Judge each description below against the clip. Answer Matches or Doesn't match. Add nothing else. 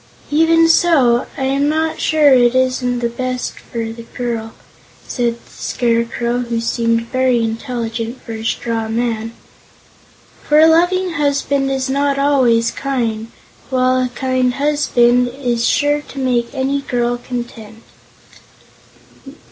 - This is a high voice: Matches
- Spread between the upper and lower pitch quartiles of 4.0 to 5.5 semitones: Doesn't match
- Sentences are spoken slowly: Matches